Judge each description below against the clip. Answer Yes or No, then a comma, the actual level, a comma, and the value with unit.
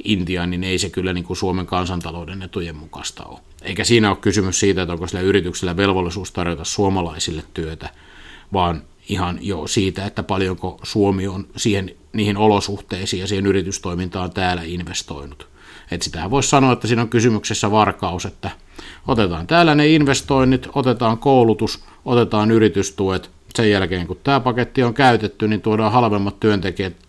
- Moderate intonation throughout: Yes, average, 3.2 semitones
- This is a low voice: Yes, very low, 95 Hz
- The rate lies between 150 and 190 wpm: Yes, fast, 155 wpm